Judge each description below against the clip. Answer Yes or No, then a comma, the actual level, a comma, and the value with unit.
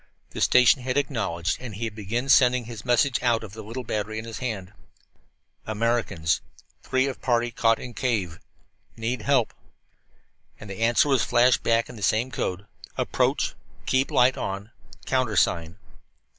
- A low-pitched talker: Yes, low, 115 Hz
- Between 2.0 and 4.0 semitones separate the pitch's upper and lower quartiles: Yes, average, 3.2 semitones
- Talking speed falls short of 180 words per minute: Yes, average, 160 wpm